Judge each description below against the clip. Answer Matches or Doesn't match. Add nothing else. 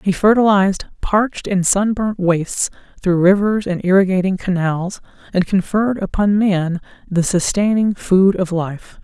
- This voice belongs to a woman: Matches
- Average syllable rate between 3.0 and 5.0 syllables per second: Matches